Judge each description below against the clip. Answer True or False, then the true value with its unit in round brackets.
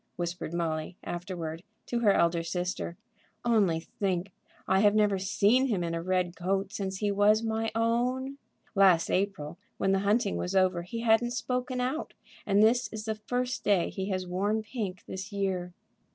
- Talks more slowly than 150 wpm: False (170 wpm)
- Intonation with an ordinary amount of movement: True (3.7 semitones)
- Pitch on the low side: False (195 Hz)